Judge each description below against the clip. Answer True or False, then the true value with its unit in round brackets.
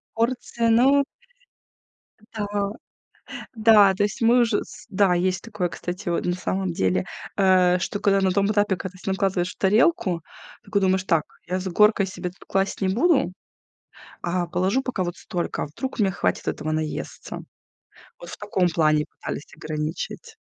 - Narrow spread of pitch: False (3.0 semitones)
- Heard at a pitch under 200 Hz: True (190 Hz)